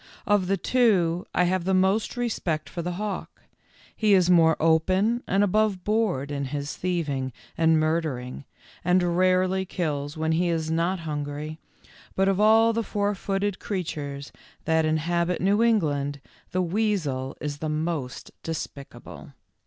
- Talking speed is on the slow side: No, average, 145 wpm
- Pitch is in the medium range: Yes, medium, 175 Hz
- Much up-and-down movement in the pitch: No, average, 4.0 semitones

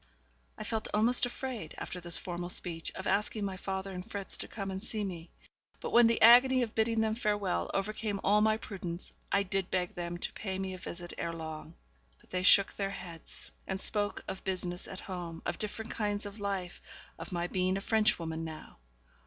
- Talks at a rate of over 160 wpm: Yes, average, 200 wpm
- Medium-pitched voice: No, high, 195 Hz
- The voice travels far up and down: No, average, 3.3 semitones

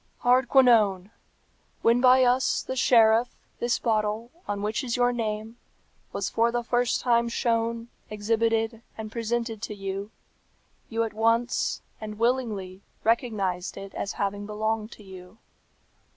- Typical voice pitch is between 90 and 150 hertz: No, high, 225 Hz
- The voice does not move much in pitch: Yes, narrow, 2.2 semitones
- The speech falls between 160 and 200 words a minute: No, slow, 135 wpm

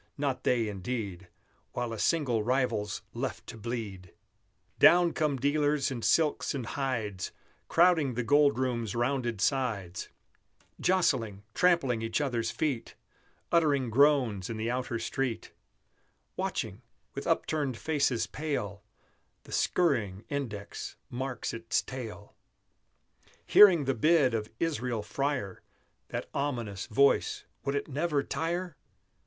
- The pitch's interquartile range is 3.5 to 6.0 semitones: Yes, average, 4.3 semitones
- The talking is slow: Yes, slow, 120 wpm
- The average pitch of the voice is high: No, low, 125 Hz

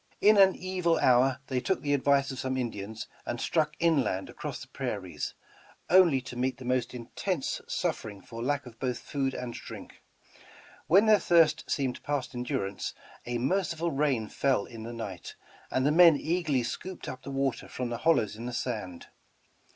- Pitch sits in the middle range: No, low, 130 Hz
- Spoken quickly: No, average, 175 wpm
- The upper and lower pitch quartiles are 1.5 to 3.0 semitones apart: No, average, 4.6 semitones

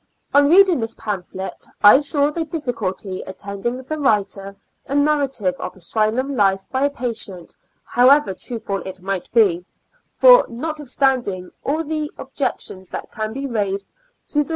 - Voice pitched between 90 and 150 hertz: No, high, 235 Hz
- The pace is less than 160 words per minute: Yes, average, 150 wpm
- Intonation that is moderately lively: No, wide, 6.5 semitones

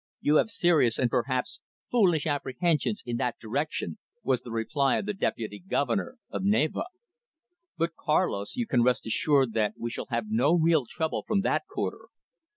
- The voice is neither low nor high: Yes, medium, 145 Hz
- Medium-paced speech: Yes, average, 165 wpm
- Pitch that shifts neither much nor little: No, wide, 6.6 semitones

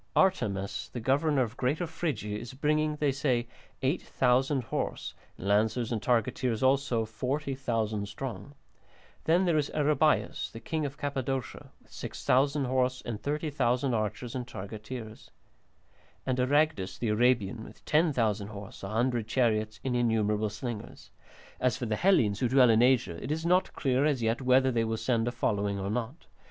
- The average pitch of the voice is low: Yes, low, 125 Hz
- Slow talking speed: No, average, 160 wpm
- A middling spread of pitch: Yes, average, 4.0 semitones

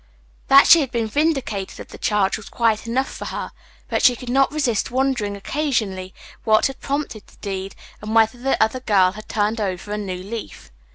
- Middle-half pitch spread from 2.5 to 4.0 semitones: No, average, 4.4 semitones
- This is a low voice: No, high, 220 Hz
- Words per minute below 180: No, average, 195 wpm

